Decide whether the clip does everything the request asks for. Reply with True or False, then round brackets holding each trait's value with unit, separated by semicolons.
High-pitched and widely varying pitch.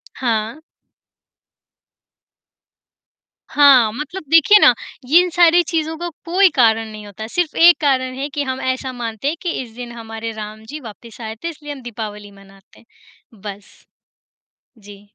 True (245 Hz; 5.7 semitones)